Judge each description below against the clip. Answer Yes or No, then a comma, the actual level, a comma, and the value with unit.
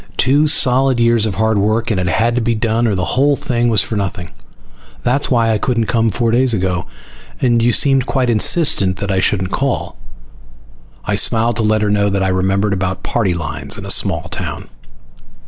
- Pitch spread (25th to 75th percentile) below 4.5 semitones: Yes, average, 3.6 semitones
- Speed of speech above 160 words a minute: Yes, average, 200 wpm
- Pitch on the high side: No, low, 110 Hz